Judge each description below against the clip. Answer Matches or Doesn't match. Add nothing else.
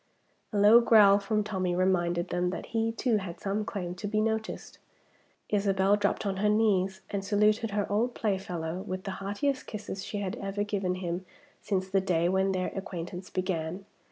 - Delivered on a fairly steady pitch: Matches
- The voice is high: Matches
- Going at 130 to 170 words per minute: Doesn't match